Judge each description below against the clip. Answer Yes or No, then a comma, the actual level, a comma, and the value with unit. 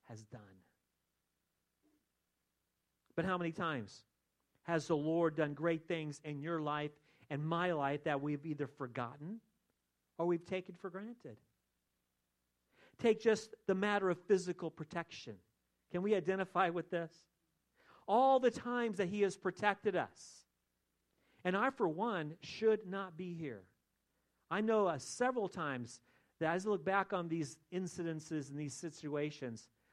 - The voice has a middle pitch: Yes, medium, 165 Hz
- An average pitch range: No, wide, 6.0 semitones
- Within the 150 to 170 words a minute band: No, average, 140 wpm